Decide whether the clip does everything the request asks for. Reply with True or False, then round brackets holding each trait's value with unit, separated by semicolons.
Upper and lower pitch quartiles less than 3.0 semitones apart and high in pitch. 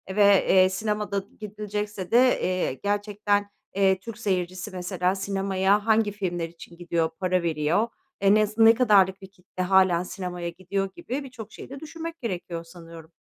True (2.6 semitones; 195 Hz)